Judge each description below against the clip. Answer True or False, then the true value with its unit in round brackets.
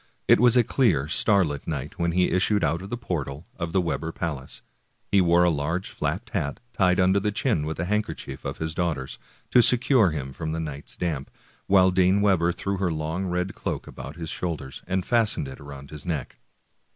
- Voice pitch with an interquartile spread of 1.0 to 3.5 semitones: False (4.2 semitones)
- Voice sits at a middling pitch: False (85 Hz)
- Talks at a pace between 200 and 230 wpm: True (205 wpm)